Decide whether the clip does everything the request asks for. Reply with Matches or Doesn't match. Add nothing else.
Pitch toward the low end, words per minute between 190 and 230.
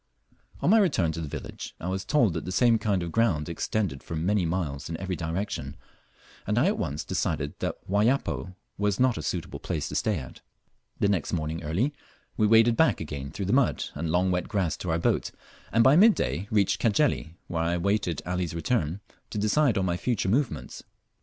Matches